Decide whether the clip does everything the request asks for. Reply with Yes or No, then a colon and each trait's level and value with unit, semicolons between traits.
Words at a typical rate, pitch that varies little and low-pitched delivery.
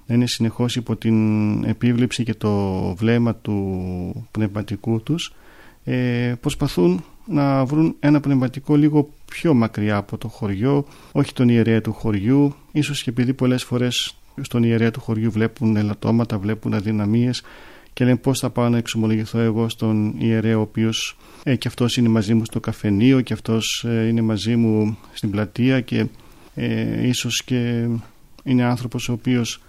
Yes: average, 155 wpm; narrow, 2.3 semitones; low, 115 Hz